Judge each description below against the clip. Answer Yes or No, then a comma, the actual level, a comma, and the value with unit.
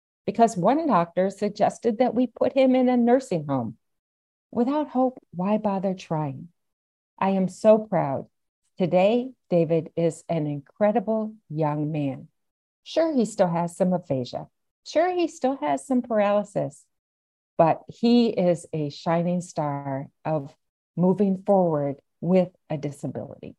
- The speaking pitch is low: No, medium, 180 Hz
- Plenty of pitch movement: Yes, wide, 6.8 semitones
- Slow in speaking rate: Yes, slow, 130 wpm